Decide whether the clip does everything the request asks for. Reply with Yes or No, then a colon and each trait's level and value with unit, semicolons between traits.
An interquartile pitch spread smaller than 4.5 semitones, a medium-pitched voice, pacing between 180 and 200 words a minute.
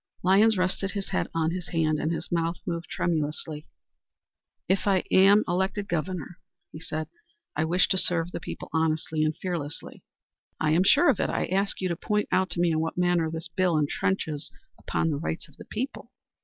Yes: average, 2.9 semitones; medium, 170 Hz; average, 195 wpm